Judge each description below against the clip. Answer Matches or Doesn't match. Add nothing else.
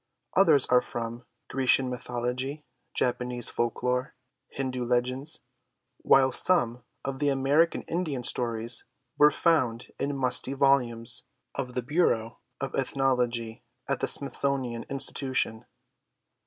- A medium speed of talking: Doesn't match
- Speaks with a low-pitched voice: Matches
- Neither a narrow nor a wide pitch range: Doesn't match